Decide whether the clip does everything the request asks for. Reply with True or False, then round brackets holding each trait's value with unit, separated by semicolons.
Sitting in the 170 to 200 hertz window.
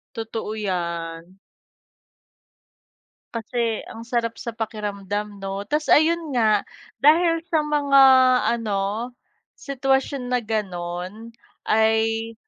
False (225 Hz)